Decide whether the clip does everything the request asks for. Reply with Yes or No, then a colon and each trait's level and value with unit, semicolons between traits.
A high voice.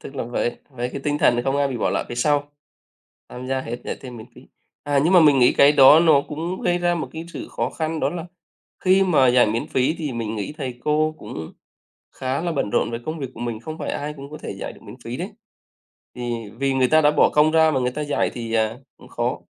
No: medium, 140 Hz